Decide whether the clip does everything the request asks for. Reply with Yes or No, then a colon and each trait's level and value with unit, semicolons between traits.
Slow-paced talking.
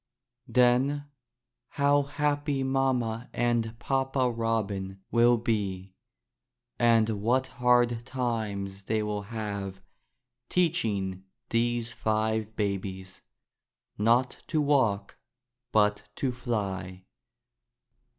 Yes: slow, 90 wpm